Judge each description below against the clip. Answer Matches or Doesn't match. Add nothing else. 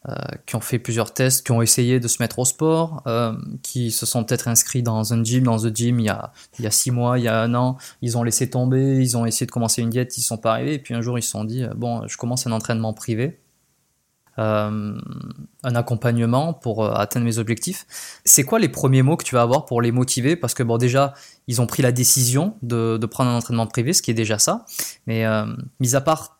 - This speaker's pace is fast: Matches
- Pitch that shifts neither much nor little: Doesn't match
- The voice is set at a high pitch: Doesn't match